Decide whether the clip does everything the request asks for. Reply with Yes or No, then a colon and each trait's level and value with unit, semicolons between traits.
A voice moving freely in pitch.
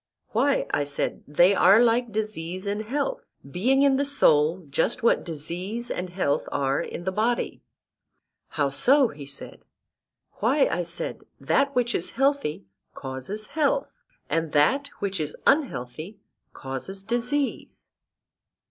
Yes: wide, 8.3 semitones